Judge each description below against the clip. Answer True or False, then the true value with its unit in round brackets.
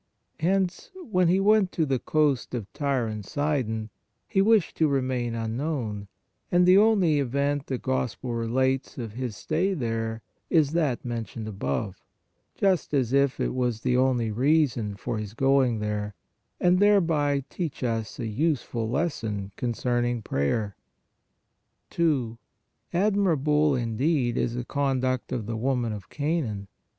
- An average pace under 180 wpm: True (140 wpm)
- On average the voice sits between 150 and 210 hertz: False (130 Hz)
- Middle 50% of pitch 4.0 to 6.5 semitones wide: True (5.3 semitones)